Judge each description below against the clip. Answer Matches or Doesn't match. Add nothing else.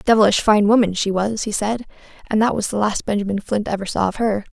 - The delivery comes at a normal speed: Doesn't match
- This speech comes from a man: Doesn't match